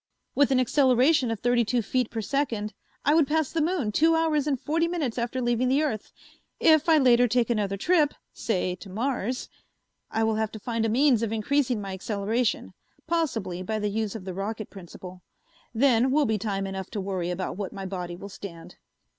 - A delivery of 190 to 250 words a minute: Yes, average, 200 wpm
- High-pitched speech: Yes, high, 230 Hz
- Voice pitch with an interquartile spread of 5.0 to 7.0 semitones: Yes, wide, 5.4 semitones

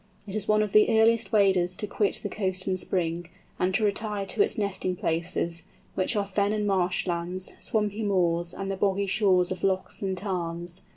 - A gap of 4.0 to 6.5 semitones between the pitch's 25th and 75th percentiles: No, narrow, 2.5 semitones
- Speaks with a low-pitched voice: No, high, 195 Hz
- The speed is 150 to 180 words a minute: No, average, 195 wpm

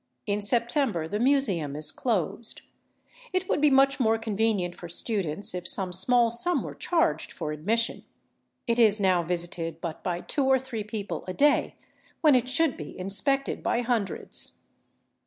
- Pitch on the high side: Yes, high, 220 Hz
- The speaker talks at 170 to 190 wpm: No, average, 160 wpm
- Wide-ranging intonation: Yes, wide, 6.3 semitones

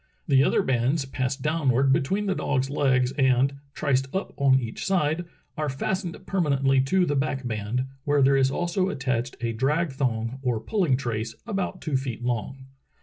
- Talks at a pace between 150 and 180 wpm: Yes, average, 170 wpm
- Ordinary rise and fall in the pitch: Yes, average, 3.0 semitones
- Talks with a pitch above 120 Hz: Yes, low, 135 Hz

